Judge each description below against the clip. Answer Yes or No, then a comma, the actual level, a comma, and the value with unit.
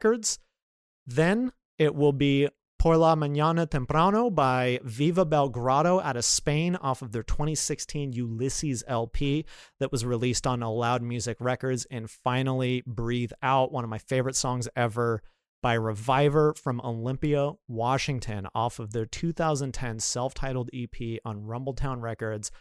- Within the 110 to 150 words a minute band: Yes, average, 140 wpm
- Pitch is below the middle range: Yes, low, 130 Hz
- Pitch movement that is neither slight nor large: Yes, average, 3.6 semitones